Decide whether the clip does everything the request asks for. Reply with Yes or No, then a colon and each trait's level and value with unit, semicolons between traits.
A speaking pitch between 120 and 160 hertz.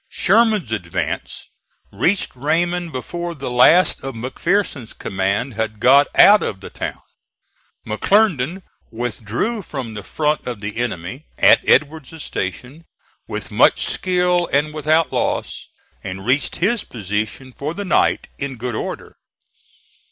Yes: medium, 140 Hz